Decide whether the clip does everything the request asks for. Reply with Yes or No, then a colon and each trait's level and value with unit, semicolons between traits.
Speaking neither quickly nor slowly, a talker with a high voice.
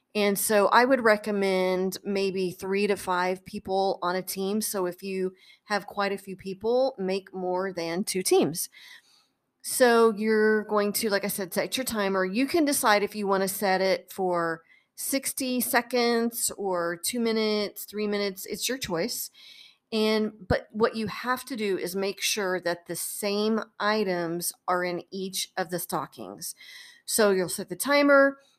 Yes: average, 170 wpm; high, 200 Hz